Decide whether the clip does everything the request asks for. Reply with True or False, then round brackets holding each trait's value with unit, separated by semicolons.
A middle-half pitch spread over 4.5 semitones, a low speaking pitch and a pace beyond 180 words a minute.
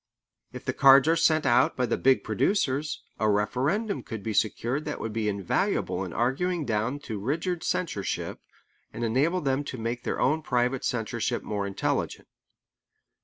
False (5.2 semitones; 130 Hz; 165 wpm)